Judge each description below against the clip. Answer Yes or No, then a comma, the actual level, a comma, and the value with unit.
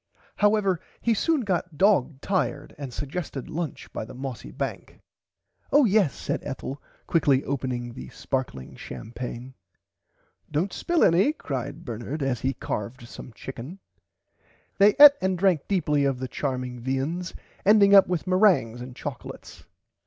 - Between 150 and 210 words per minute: No, average, 140 wpm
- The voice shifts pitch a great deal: Yes, wide, 6.8 semitones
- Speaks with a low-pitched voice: No, medium, 145 Hz